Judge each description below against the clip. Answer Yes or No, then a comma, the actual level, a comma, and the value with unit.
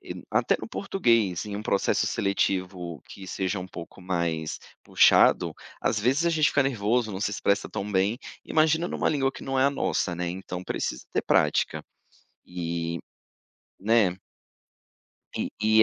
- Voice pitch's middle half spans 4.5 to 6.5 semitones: Yes, wide, 5.5 semitones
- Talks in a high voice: No, low, 100 Hz